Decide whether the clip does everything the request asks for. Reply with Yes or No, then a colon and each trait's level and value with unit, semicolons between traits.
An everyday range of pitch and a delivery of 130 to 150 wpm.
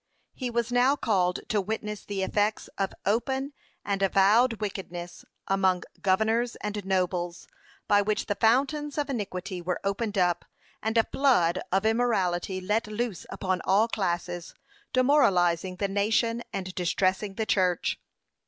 Yes: average, 3.6 semitones; average, 140 wpm